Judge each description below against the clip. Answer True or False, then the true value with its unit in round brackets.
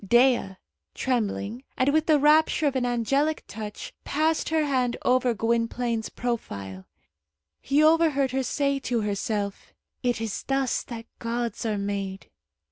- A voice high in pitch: True (245 Hz)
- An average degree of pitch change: True (4.0 semitones)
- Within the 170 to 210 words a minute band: False (135 wpm)